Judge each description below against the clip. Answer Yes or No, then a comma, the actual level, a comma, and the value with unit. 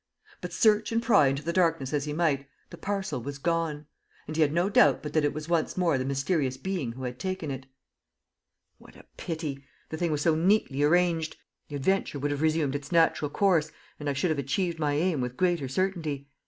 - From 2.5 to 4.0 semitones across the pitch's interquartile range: Yes, average, 3.7 semitones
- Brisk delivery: Yes, fast, 215 wpm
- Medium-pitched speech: Yes, medium, 155 Hz